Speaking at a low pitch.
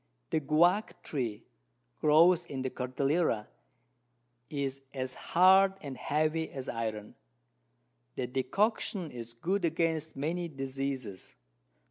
No: medium, 145 Hz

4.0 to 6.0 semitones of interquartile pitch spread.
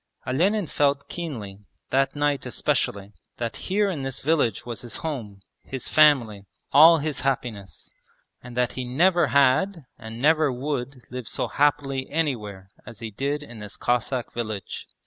Yes: average, 4.3 semitones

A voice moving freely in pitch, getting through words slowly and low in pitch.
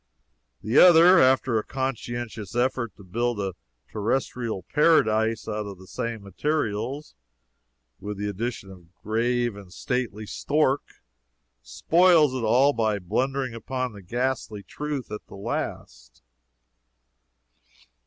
No: average, 4.3 semitones; slow, 125 wpm; low, 115 Hz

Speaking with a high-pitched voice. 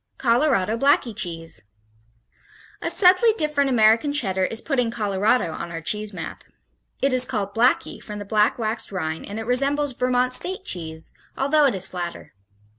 Yes: high, 225 Hz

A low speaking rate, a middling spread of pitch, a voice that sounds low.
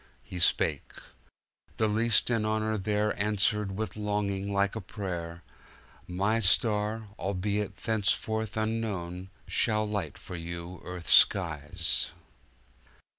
Yes: slow, 105 wpm; average, 3.0 semitones; low, 105 Hz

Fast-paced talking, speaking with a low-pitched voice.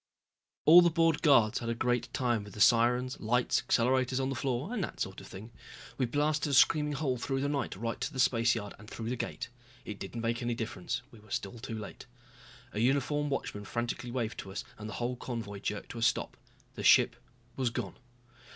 Yes: fast, 215 wpm; low, 120 Hz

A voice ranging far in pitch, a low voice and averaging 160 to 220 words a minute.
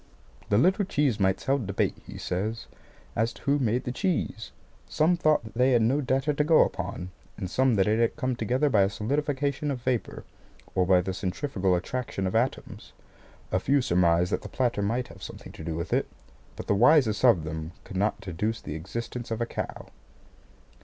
Yes: wide, 5.7 semitones; low, 115 Hz; average, 200 wpm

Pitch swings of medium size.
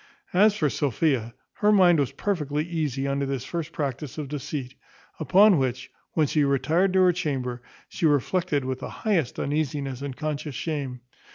Yes: average, 3.7 semitones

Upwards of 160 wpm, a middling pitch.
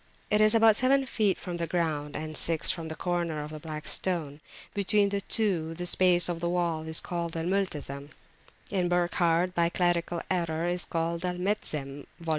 Yes: average, 180 wpm; medium, 175 Hz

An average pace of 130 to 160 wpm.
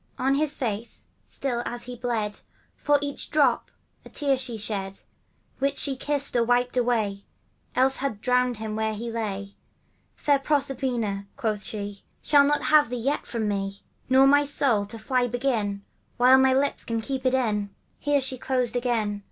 No: average, 180 wpm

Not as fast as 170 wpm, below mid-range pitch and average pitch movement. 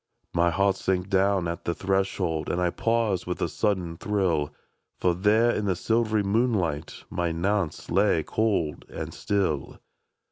Yes: average, 150 wpm; very low, 95 Hz; average, 3.4 semitones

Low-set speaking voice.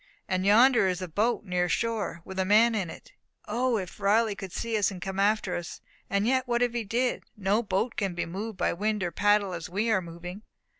No: high, 205 Hz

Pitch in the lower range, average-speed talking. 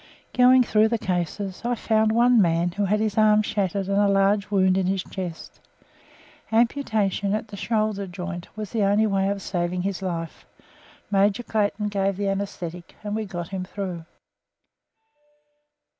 No: high, 200 Hz; average, 160 wpm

